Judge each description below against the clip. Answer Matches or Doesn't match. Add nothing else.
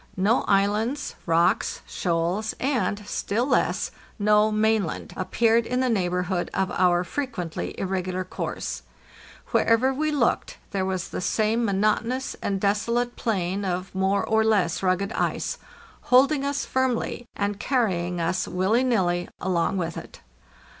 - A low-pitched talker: Doesn't match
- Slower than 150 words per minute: Matches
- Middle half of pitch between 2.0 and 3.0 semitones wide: Doesn't match